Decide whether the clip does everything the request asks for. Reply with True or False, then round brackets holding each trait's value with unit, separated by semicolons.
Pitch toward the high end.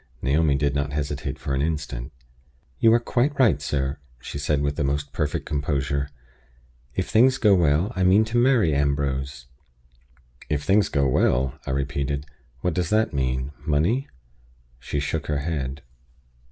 False (70 Hz)